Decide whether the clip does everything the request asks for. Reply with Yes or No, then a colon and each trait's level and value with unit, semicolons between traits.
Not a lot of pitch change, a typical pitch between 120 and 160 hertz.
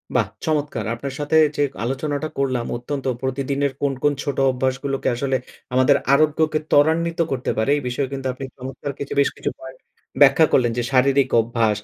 Yes: narrow, 2.0 semitones; low, 135 Hz